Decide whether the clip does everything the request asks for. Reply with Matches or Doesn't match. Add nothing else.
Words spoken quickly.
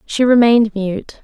Doesn't match